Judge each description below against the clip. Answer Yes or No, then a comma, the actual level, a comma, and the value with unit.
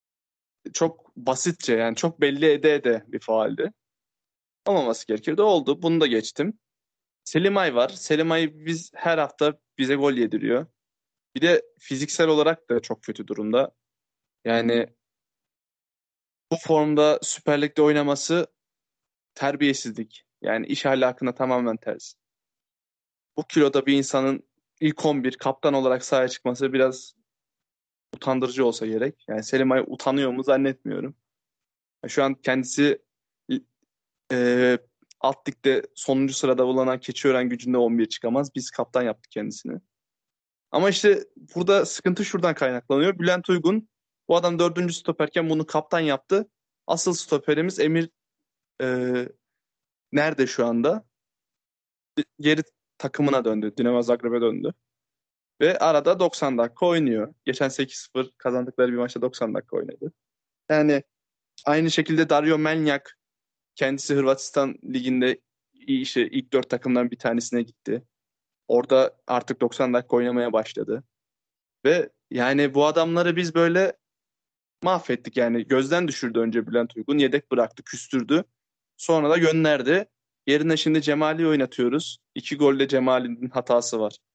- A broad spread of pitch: No, average, 4.3 semitones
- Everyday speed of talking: Yes, average, 120 wpm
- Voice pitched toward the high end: No, low, 135 Hz